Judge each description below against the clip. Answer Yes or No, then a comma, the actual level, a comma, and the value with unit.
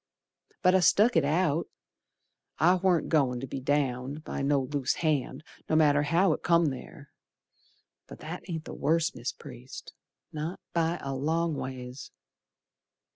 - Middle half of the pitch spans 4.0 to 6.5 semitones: No, average, 3.5 semitones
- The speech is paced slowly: No, average, 150 wpm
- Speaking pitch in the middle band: Yes, medium, 155 Hz